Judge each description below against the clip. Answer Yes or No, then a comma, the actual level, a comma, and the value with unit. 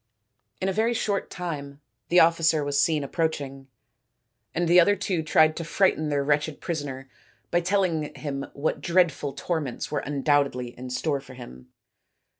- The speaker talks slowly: No, average, 160 wpm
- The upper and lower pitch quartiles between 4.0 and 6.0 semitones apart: No, average, 3.5 semitones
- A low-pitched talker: No, medium, 155 Hz